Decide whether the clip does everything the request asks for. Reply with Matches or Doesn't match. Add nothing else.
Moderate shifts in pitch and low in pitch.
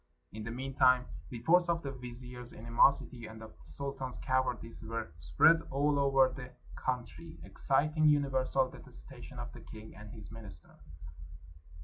Matches